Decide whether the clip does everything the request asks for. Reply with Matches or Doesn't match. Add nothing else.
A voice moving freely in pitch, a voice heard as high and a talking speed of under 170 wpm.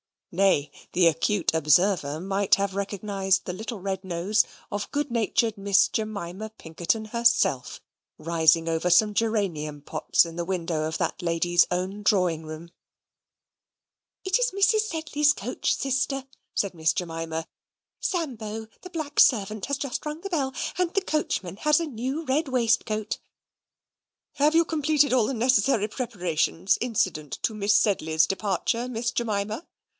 Matches